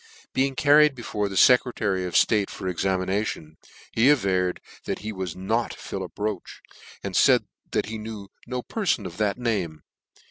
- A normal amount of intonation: Yes, average, 4.4 semitones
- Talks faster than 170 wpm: No, average, 165 wpm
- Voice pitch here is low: Yes, low, 105 Hz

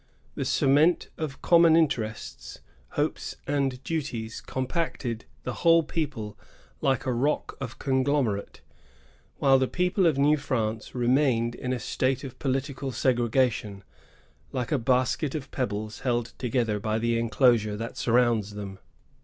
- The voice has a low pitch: Yes, low, 130 Hz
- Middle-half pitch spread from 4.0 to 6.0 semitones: No, average, 3.5 semitones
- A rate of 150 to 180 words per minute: No, slow, 135 wpm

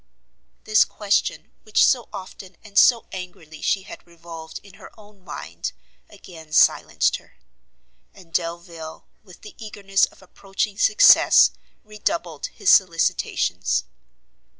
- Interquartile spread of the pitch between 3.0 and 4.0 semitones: Yes, average, 3.7 semitones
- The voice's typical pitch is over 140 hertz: Yes, high, 190 Hz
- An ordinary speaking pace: No, slow, 120 wpm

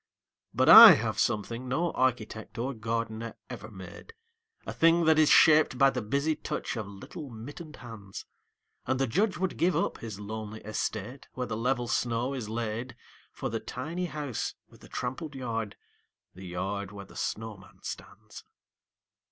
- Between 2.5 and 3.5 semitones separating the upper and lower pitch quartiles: No, average, 4.2 semitones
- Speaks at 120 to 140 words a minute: No, average, 160 wpm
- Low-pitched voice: Yes, low, 115 Hz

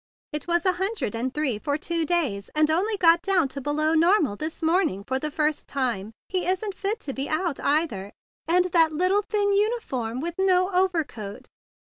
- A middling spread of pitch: Yes, average, 4.9 semitones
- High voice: Yes, very high, 325 Hz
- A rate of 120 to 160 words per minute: No, average, 190 wpm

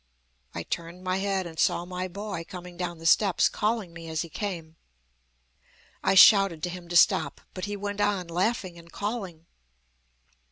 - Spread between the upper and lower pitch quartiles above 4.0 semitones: No, average, 2.9 semitones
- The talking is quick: No, average, 170 wpm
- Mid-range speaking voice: Yes, medium, 180 Hz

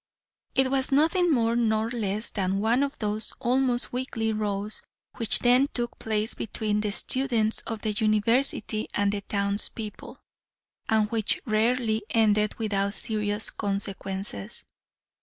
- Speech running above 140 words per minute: No, slow, 135 wpm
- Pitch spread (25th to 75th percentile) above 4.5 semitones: No, narrow, 2.6 semitones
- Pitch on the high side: Yes, high, 220 Hz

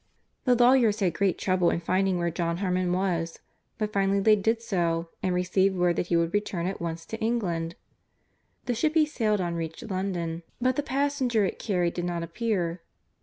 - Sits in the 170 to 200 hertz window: Yes, medium, 185 Hz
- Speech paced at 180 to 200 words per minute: Yes, average, 190 wpm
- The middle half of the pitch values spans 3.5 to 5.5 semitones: Yes, average, 4.4 semitones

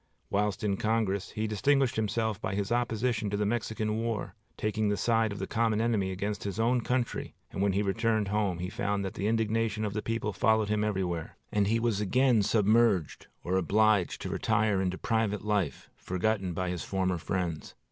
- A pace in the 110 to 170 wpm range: No, average, 190 wpm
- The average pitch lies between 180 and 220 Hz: No, low, 105 Hz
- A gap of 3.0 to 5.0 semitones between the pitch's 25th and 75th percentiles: No, narrow, 2.4 semitones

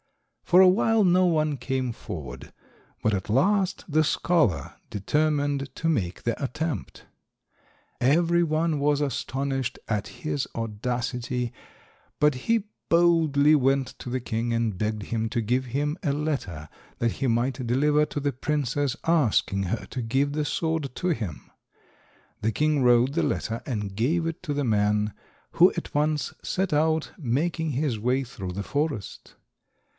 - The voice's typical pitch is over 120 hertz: Yes, low, 135 Hz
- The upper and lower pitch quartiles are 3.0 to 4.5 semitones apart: No, average, 4.9 semitones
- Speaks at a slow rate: No, average, 150 wpm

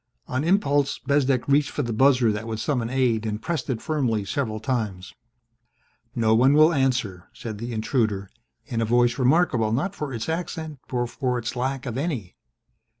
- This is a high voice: No, low, 125 Hz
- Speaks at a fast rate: No, average, 175 wpm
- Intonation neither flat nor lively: Yes, average, 4.1 semitones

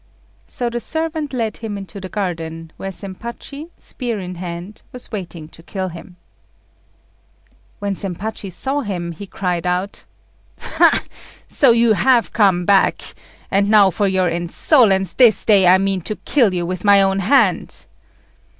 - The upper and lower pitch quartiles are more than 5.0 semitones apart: No, average, 3.9 semitones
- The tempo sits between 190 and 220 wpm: No, average, 150 wpm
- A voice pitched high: Yes, high, 195 Hz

